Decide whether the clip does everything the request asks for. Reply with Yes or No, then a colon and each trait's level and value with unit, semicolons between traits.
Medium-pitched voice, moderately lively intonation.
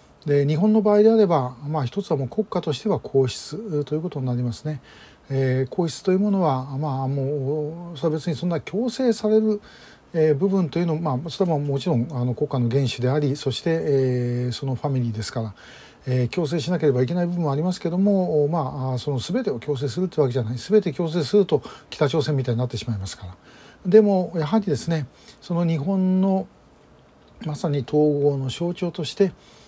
Yes: medium, 150 Hz; average, 5.0 semitones